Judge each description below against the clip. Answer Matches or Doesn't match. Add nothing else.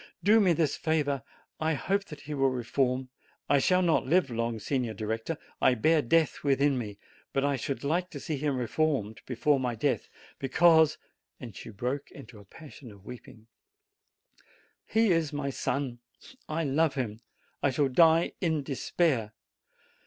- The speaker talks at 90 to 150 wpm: Doesn't match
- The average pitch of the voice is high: Doesn't match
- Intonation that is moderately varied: Matches